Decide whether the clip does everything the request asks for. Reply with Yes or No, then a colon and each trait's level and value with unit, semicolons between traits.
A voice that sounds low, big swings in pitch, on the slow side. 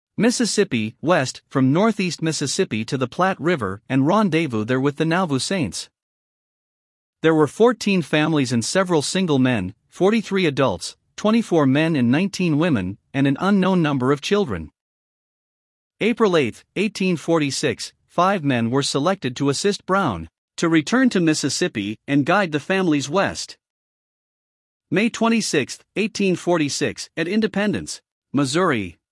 No: medium, 160 Hz; wide, 5.8 semitones; slow, 130 wpm